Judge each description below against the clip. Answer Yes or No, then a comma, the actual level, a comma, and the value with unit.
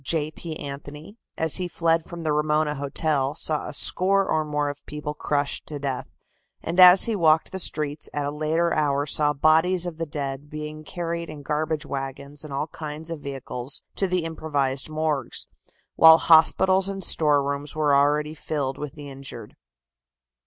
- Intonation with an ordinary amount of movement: No, narrow, 2.1 semitones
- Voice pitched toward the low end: No, medium, 150 Hz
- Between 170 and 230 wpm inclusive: Yes, average, 175 wpm